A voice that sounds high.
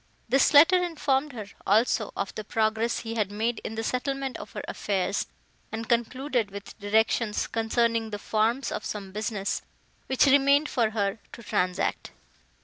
Yes: high, 225 Hz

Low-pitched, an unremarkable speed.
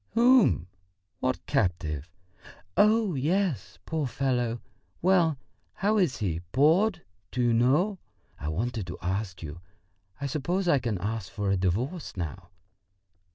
No: low, 125 Hz; slow, 130 wpm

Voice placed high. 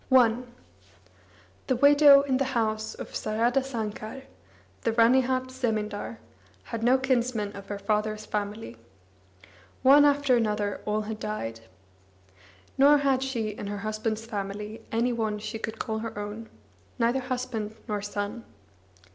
Yes: high, 225 Hz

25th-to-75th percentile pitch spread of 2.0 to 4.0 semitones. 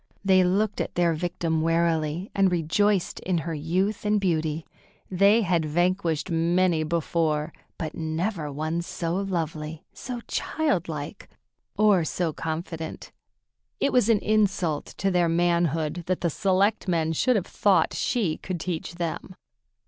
Yes: average, 3.2 semitones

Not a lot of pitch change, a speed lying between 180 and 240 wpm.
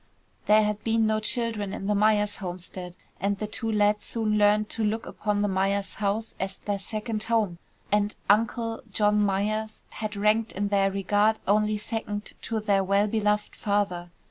No: narrow, 1.3 semitones; average, 170 wpm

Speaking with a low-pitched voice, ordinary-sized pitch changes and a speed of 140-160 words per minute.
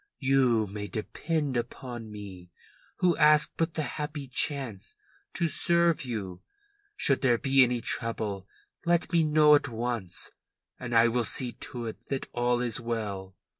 Yes: low, 125 Hz; average, 4.8 semitones; average, 150 wpm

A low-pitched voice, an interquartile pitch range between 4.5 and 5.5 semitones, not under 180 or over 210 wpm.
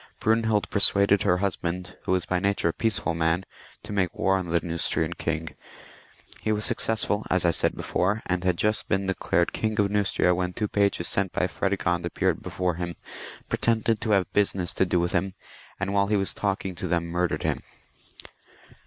No: very low, 95 Hz; average, 2.7 semitones; average, 190 wpm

